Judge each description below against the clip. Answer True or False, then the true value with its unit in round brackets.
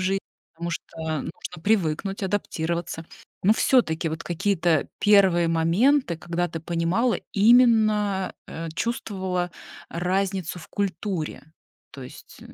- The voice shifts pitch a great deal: False (3.5 semitones)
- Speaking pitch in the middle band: True (180 Hz)